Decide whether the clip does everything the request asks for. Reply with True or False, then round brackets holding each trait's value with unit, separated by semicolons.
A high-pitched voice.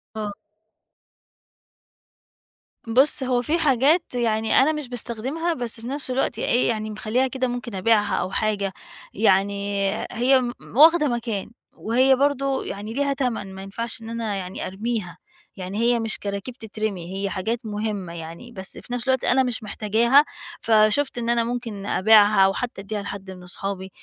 True (225 Hz)